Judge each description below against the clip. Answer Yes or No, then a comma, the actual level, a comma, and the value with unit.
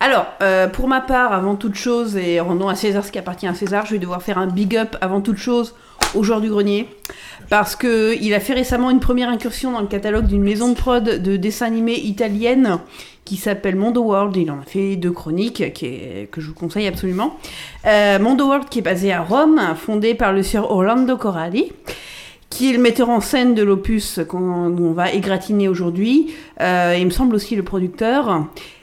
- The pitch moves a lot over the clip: No, average, 3.9 semitones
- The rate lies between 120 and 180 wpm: No, average, 210 wpm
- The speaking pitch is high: Yes, high, 210 Hz